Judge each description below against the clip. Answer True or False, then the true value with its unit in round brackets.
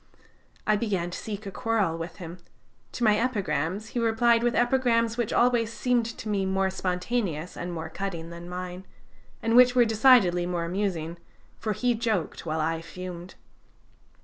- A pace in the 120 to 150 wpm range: False (165 wpm)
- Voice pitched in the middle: False (195 Hz)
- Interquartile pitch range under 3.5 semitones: False (4.8 semitones)